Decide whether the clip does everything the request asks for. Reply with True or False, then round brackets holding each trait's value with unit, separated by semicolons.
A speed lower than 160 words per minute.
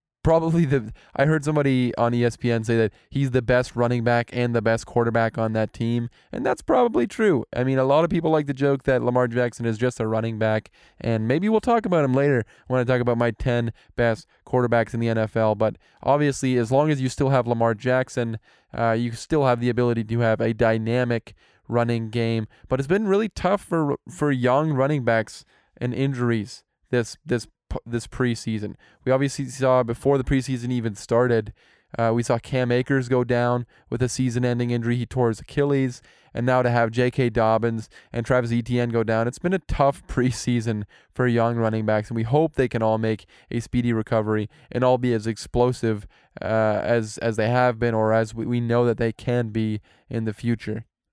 False (205 wpm)